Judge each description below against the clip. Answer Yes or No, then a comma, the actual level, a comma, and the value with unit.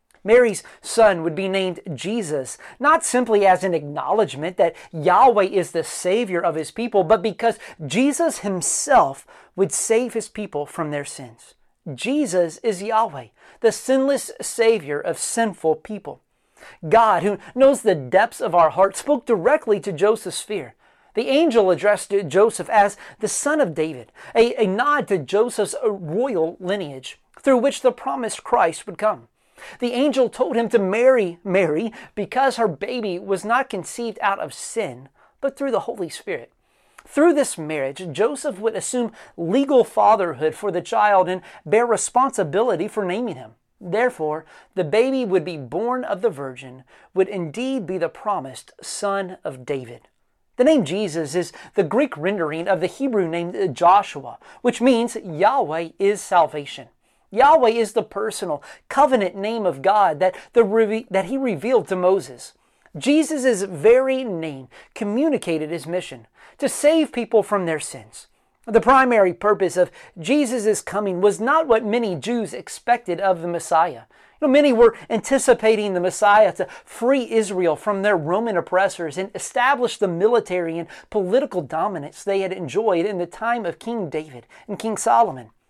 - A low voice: No, high, 205 Hz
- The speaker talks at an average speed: Yes, average, 155 wpm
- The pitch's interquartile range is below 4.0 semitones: No, average, 5.1 semitones